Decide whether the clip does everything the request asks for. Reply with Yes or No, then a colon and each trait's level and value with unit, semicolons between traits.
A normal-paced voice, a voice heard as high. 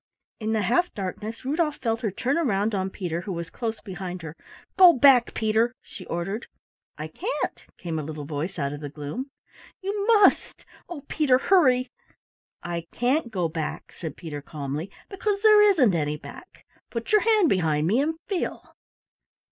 Yes: average, 170 wpm; high, 220 Hz